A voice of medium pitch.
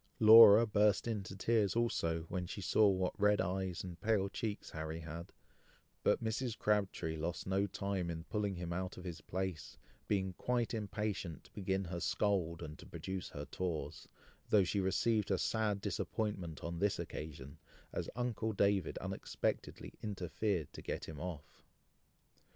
No: very low, 95 Hz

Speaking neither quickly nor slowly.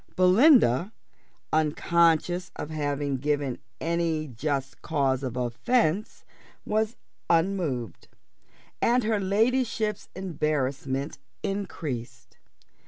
No: slow, 80 wpm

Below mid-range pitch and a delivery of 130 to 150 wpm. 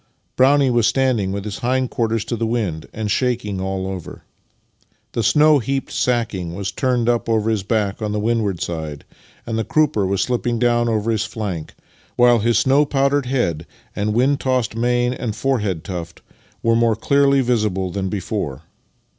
No: low, 115 Hz; average, 170 wpm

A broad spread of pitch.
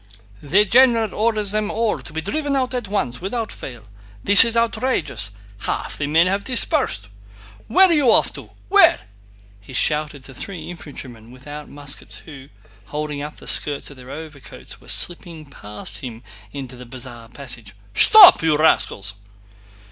Yes: wide, 8.8 semitones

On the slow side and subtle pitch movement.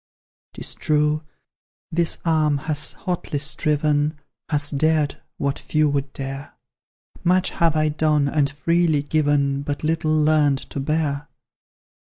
Yes: slow, 125 wpm; narrow, 1.5 semitones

